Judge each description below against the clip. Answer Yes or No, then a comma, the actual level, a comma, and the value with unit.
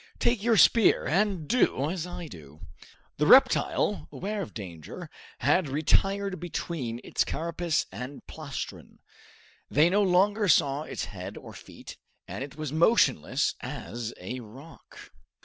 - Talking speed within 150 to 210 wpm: No, slow, 135 wpm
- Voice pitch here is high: No, medium, 160 Hz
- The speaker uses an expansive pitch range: Yes, wide, 7.0 semitones